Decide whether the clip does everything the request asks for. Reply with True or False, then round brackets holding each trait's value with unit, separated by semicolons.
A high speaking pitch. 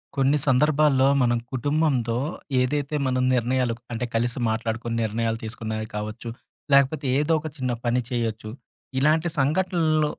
False (125 Hz)